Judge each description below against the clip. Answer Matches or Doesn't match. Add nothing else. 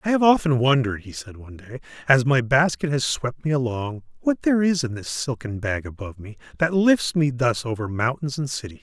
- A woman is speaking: Doesn't match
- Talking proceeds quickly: Matches